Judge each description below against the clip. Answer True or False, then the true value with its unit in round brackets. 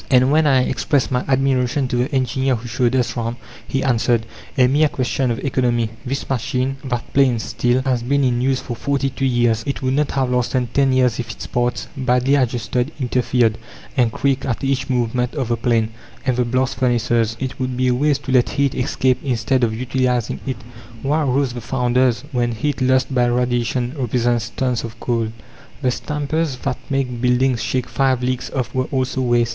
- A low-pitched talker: True (125 Hz)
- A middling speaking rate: True (195 wpm)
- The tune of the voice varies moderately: False (1.7 semitones)